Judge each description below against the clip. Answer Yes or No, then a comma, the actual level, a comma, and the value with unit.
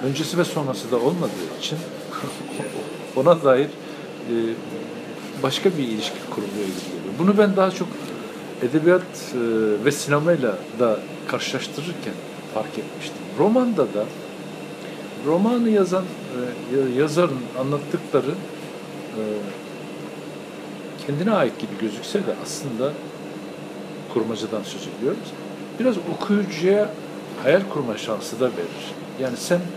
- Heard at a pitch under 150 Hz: No, medium, 155 Hz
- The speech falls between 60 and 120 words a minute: Yes, average, 105 wpm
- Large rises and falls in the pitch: Yes, wide, 6.8 semitones